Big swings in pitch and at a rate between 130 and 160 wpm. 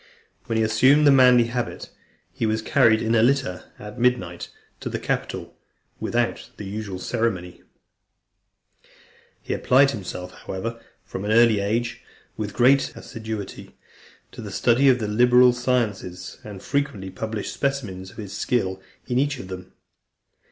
No: average, 3.9 semitones; average, 150 wpm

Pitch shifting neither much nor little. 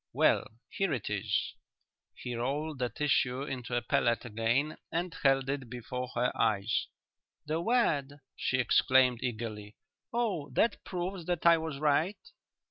Yes: average, 4.8 semitones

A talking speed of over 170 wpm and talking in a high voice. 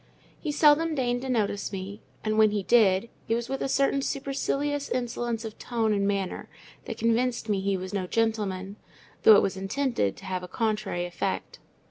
Yes: average, 185 wpm; high, 220 Hz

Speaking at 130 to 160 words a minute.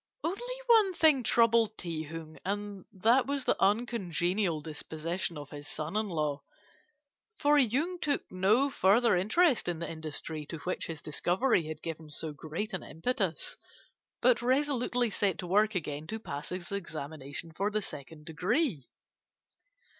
Yes: average, 150 wpm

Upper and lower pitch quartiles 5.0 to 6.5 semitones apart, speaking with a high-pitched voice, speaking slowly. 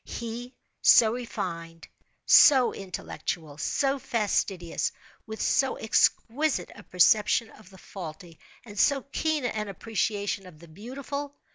Yes: wide, 5.6 semitones; high, 215 Hz; slow, 120 wpm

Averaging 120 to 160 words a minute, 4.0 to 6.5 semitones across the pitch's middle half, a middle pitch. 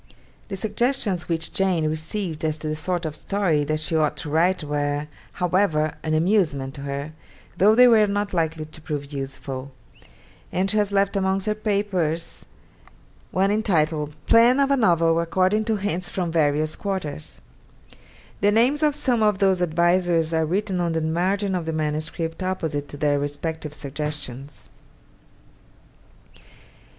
Yes: average, 155 wpm; average, 4.4 semitones; medium, 170 Hz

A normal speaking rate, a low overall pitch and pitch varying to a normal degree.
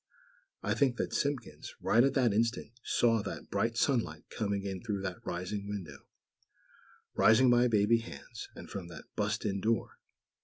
Yes: average, 160 wpm; low, 110 Hz; average, 3.0 semitones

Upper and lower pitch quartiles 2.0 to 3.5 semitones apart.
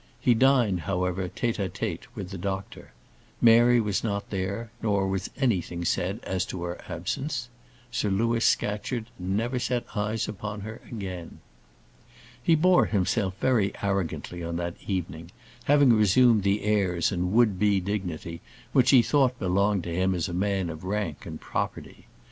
No: average, 3.9 semitones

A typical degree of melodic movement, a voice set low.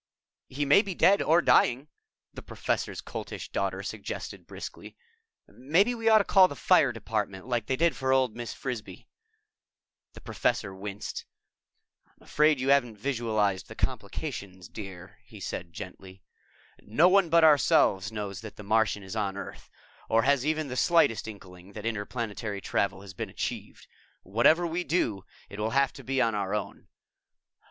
No: wide, 6.3 semitones; low, 115 Hz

